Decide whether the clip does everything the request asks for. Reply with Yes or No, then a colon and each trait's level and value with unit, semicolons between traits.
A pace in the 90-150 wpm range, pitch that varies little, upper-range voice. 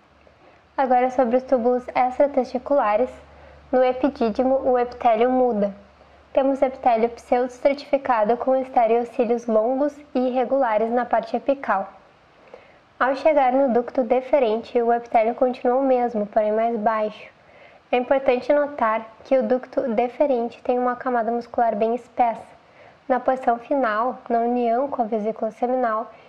Yes: average, 130 wpm; narrow, 2.1 semitones; very high, 250 Hz